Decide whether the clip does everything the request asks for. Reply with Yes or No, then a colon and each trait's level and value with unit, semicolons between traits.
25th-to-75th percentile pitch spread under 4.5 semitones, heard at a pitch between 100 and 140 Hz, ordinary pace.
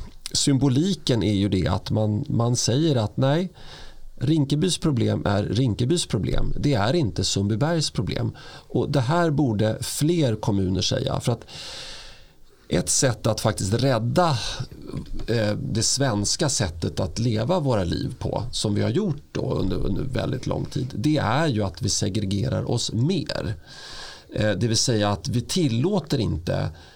No: average, 5.2 semitones; low, 120 Hz; average, 150 wpm